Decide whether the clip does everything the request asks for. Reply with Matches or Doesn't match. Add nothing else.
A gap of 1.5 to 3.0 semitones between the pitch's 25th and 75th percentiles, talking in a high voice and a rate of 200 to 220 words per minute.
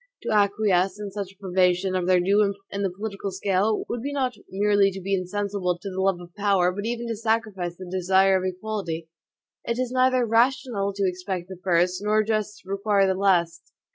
Matches